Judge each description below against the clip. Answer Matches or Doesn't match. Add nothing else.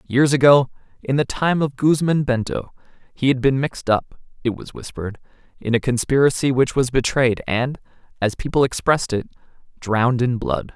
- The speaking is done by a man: Matches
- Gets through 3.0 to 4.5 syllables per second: Doesn't match